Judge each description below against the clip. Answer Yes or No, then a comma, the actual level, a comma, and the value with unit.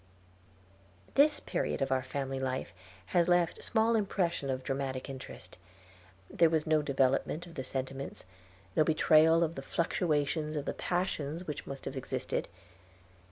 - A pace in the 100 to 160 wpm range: Yes, average, 145 wpm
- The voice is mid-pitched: Yes, medium, 150 Hz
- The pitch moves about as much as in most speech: Yes, average, 3.9 semitones